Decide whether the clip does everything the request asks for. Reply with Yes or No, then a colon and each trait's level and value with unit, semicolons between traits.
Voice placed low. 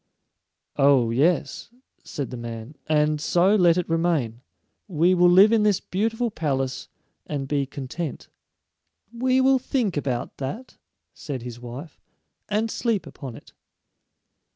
No: medium, 155 Hz